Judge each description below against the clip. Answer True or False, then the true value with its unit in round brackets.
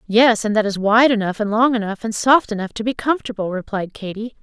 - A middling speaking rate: False (230 wpm)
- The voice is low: False (220 Hz)